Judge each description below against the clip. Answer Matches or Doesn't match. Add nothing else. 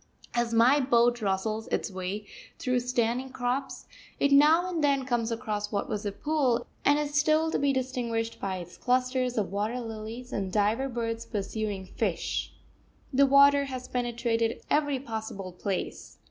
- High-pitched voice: Matches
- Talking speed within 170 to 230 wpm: Doesn't match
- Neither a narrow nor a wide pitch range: Matches